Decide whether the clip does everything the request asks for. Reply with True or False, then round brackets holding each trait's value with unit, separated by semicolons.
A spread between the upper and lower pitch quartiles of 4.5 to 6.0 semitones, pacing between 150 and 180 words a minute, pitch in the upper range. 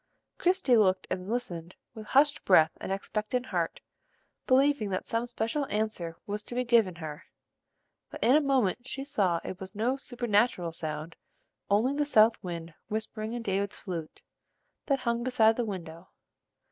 True (5.1 semitones; 160 wpm; 220 Hz)